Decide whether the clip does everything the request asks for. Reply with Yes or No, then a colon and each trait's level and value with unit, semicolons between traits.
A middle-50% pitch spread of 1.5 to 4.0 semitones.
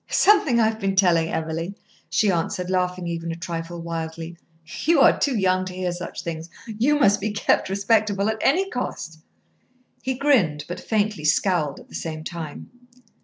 No: average, 4.7 semitones